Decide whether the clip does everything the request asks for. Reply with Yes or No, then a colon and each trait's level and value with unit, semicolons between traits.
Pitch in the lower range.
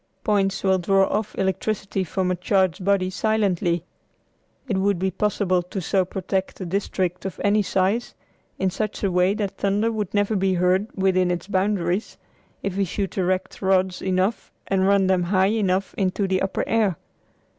No: high, 190 Hz